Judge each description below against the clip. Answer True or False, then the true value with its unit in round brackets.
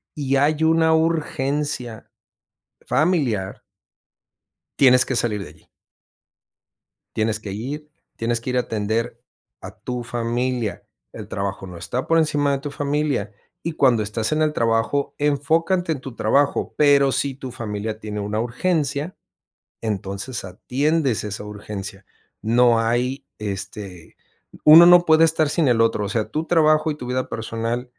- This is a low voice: True (125 Hz)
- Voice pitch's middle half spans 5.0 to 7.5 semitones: True (5.3 semitones)